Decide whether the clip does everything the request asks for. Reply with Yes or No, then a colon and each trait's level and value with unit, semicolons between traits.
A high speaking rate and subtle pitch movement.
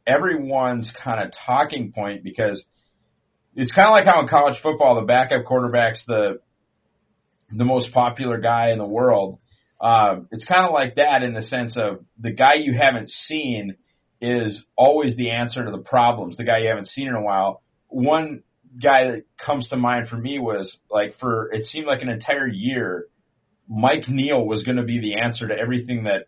No: average, 190 wpm; narrow, 2.3 semitones